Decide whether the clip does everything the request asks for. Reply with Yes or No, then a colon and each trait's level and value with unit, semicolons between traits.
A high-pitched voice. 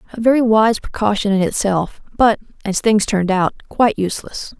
Yes: high, 210 Hz